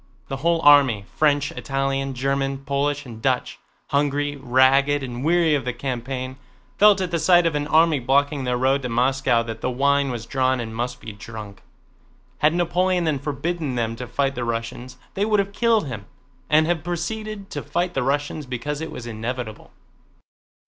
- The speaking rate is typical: Yes, average, 175 wpm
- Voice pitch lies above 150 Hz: No, low, 135 Hz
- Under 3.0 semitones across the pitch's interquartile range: No, average, 3.8 semitones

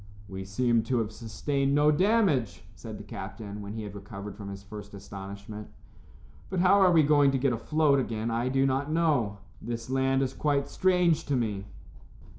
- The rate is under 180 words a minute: No, average, 185 wpm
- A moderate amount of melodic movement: No, wide, 5.8 semitones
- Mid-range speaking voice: No, low, 125 Hz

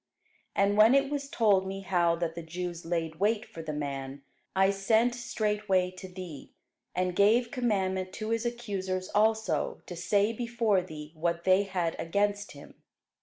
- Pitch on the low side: No, high, 190 Hz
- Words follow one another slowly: No, average, 165 wpm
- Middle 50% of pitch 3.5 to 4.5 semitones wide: Yes, average, 3.9 semitones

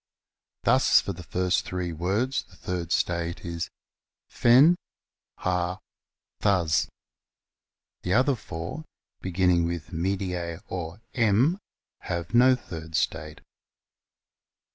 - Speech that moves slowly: Yes, slow, 100 wpm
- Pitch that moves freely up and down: No, average, 3.5 semitones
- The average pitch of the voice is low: Yes, very low, 90 Hz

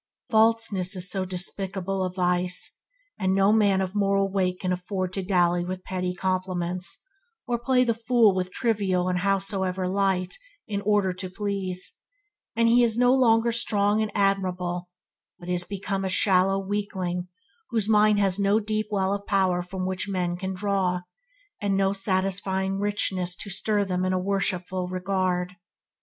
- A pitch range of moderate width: No, narrow, 1.9 semitones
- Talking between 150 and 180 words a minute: Yes, average, 160 wpm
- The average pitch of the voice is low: No, high, 190 Hz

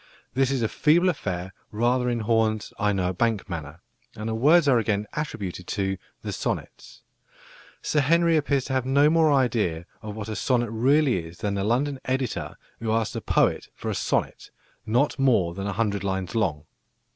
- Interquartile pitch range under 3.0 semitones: No, average, 5.2 semitones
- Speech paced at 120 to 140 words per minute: No, average, 190 wpm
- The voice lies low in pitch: Yes, low, 115 Hz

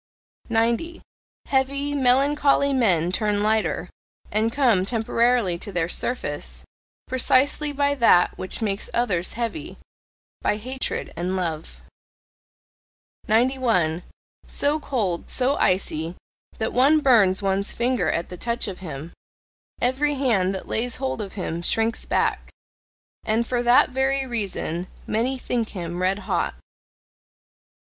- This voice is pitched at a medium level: No, high, 230 Hz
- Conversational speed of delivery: No, slow, 125 wpm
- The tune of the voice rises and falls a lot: Yes, wide, 5.8 semitones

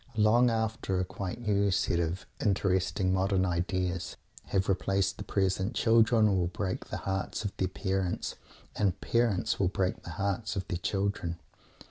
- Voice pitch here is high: No, very low, 95 Hz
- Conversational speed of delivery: Yes, average, 155 wpm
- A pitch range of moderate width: No, narrow, 2.2 semitones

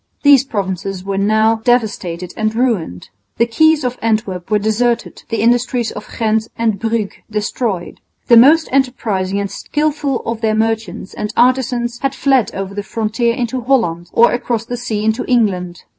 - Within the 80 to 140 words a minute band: No, average, 160 wpm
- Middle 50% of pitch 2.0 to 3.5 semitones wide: Yes, average, 3.0 semitones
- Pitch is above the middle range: Yes, high, 225 Hz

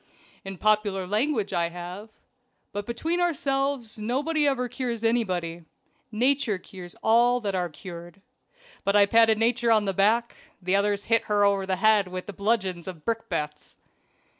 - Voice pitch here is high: Yes, high, 210 Hz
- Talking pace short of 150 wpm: No, average, 155 wpm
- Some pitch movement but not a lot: Yes, average, 3.9 semitones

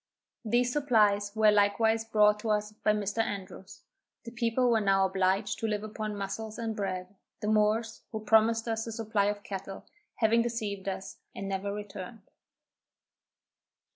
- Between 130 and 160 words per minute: Yes, average, 150 wpm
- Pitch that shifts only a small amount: Yes, narrow, 1.9 semitones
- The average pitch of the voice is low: No, high, 210 Hz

